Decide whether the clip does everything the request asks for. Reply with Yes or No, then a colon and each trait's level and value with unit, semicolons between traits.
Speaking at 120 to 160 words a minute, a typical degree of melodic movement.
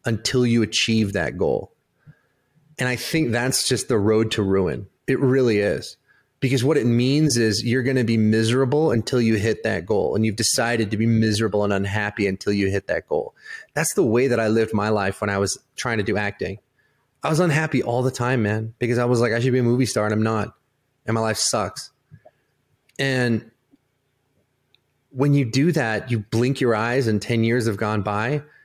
No: fast, 205 wpm; average, 3.5 semitones